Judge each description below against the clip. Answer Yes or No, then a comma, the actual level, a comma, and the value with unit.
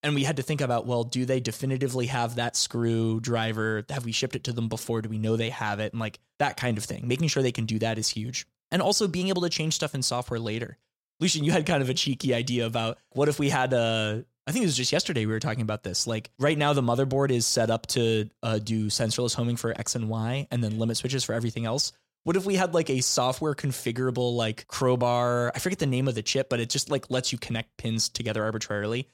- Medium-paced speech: No, fast, 260 wpm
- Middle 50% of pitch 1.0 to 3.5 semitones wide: Yes, average, 3.1 semitones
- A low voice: Yes, low, 120 Hz